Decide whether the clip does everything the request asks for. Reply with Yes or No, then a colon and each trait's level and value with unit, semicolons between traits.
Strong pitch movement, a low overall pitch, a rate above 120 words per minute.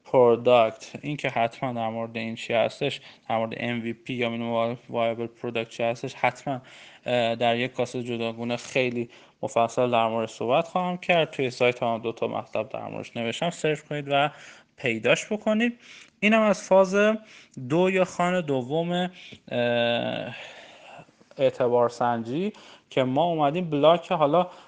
Yes: wide, 6.4 semitones; low, 125 Hz; average, 140 wpm